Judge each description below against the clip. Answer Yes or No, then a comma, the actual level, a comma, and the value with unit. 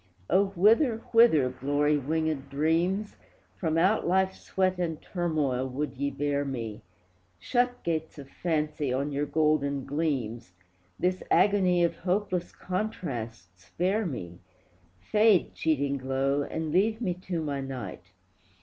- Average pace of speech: No, slow, 130 wpm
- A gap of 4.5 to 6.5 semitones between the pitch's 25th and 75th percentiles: Yes, average, 5.0 semitones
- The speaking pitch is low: No, medium, 155 Hz